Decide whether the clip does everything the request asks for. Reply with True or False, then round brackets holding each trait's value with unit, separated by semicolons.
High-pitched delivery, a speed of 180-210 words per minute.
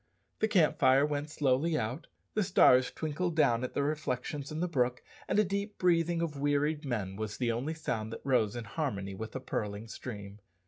False (140 Hz; 195 wpm)